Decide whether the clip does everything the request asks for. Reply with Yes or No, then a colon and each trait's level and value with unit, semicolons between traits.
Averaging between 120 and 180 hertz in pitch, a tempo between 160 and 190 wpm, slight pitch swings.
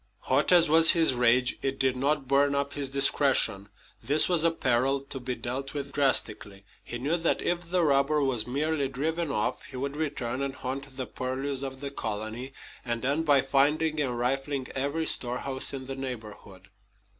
Yes: low, 135 Hz; average, 180 wpm; narrow, 2.3 semitones